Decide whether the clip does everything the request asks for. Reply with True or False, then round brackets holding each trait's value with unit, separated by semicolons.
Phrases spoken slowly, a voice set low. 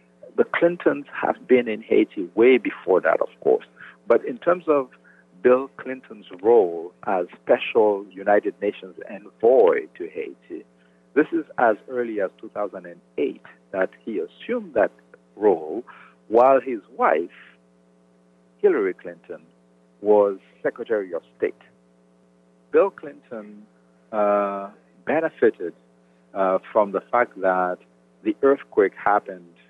True (115 wpm; 100 Hz)